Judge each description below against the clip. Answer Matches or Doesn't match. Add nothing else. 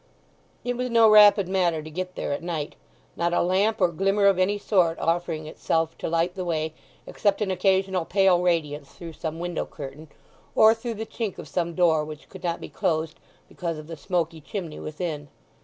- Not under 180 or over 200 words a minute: Matches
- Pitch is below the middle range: Doesn't match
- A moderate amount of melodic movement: Matches